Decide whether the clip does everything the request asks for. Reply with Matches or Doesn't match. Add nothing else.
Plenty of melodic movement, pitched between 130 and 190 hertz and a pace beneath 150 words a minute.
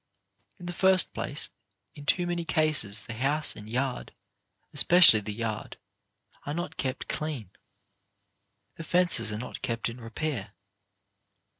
Matches